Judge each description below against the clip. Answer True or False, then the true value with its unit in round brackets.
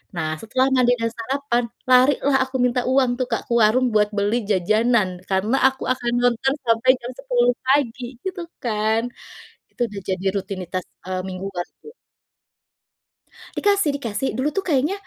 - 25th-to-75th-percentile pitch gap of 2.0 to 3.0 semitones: False (3.9 semitones)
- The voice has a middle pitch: False (240 Hz)